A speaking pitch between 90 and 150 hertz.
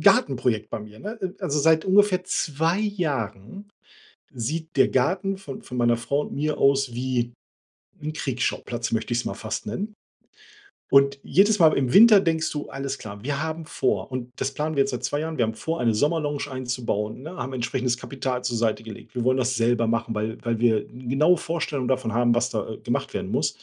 Yes: low, 135 Hz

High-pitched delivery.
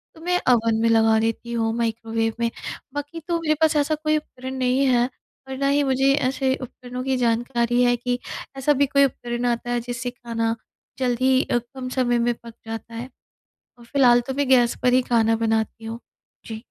Yes: high, 245 Hz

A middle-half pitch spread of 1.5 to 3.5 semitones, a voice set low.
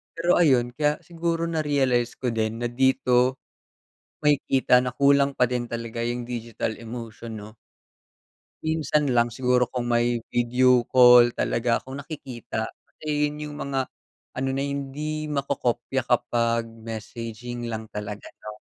Yes: average, 3.0 semitones; low, 125 Hz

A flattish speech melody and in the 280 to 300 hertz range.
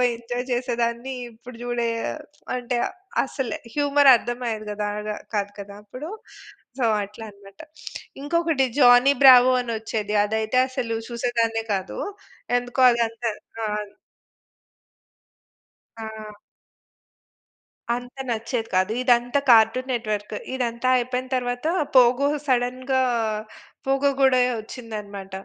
No: narrow, 2.3 semitones; high, 240 Hz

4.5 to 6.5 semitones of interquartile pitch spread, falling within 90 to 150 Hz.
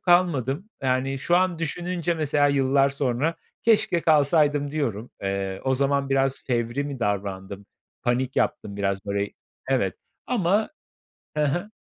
Yes: wide, 5.5 semitones; medium, 140 Hz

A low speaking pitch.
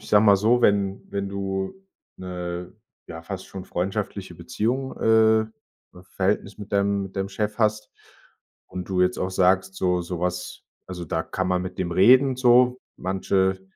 Yes: very low, 95 Hz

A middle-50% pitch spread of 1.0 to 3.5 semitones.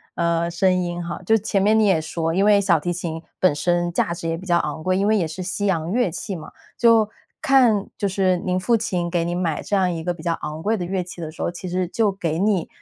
Yes: average, 2.8 semitones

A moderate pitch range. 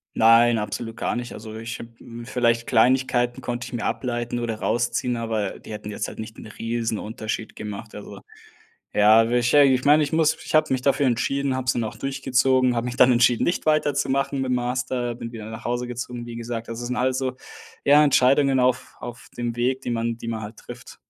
No: narrow, 2.1 semitones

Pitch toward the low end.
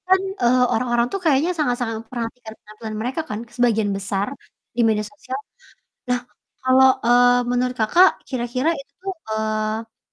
No: high, 245 Hz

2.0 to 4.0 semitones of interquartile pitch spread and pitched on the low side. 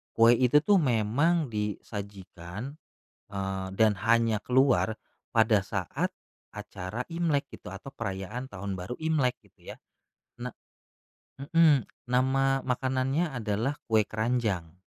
No: average, 4.8 semitones; low, 115 Hz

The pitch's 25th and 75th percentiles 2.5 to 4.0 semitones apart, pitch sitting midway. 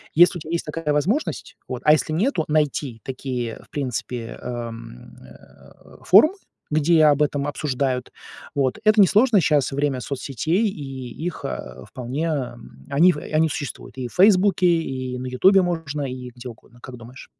No: average, 4.7 semitones; medium, 145 Hz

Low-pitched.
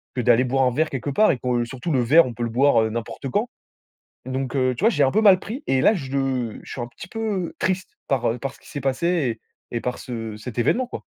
Yes: low, 130 Hz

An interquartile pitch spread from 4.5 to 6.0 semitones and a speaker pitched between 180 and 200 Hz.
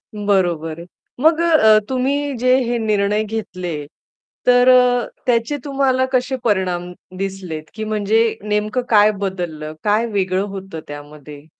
No: average, 5.2 semitones; high, 210 Hz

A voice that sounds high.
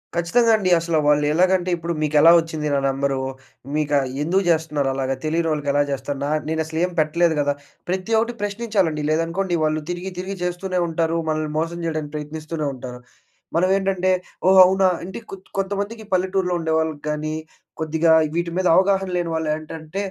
No: medium, 165 Hz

